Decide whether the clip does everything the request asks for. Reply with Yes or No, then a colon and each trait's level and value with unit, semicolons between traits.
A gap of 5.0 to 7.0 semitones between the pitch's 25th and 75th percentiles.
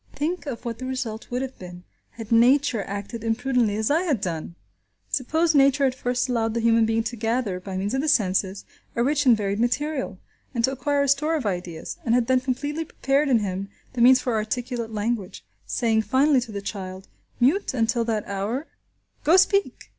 No: average, 4.0 semitones